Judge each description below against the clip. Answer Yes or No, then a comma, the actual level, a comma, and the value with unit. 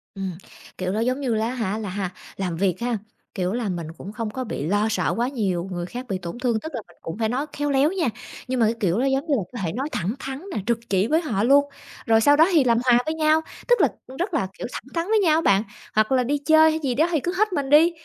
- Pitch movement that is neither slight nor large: No, wide, 6.2 semitones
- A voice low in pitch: No, high, 245 Hz